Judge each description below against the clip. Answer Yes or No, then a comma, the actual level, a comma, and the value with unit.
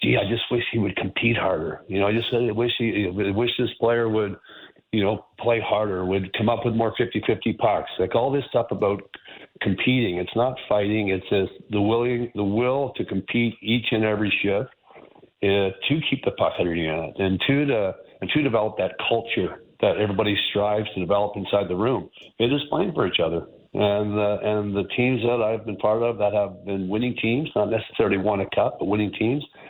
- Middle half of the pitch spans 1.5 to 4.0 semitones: Yes, average, 2.9 semitones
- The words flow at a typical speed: No, fast, 210 wpm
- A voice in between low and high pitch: No, low, 105 Hz